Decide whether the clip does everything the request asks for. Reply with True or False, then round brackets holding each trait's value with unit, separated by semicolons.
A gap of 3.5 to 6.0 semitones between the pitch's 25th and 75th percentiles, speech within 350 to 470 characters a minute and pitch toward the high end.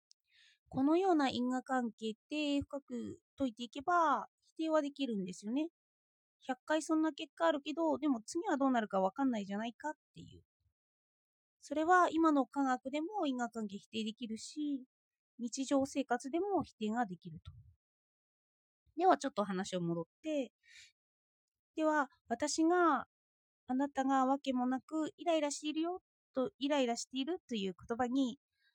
False (5.2 semitones; 300 characters per minute; 270 Hz)